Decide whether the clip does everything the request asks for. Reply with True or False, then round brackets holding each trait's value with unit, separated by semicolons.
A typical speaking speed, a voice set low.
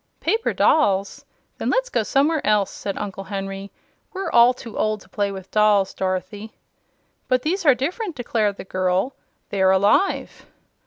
False (155 wpm; 210 Hz)